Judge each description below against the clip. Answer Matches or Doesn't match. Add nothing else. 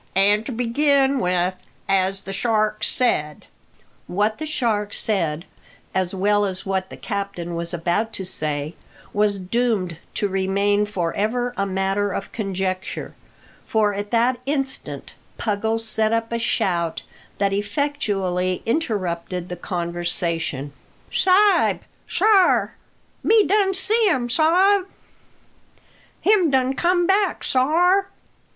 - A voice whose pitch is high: Matches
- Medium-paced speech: Doesn't match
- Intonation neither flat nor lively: Doesn't match